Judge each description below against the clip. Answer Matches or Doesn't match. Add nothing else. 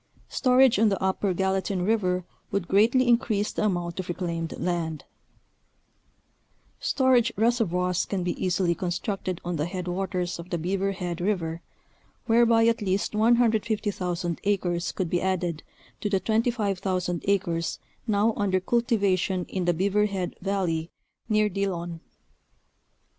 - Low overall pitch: Doesn't match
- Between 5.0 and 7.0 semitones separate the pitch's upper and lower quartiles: Doesn't match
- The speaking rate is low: Matches